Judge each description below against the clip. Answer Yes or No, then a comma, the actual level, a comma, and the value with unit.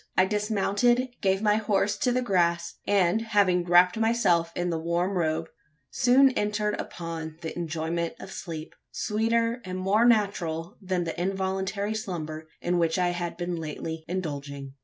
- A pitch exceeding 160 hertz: Yes, medium, 185 Hz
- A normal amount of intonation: Yes, average, 3.8 semitones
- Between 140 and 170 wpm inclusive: Yes, average, 155 wpm